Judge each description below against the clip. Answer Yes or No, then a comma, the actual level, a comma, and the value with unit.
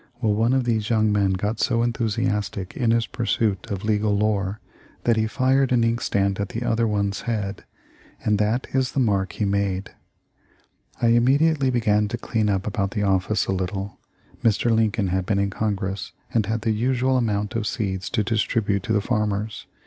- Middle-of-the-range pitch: No, low, 105 Hz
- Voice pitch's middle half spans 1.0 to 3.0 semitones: Yes, narrow, 2.6 semitones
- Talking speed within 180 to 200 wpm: Yes, average, 185 wpm